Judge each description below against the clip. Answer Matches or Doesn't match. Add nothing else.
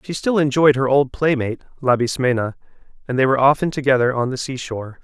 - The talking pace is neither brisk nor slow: Matches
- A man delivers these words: Matches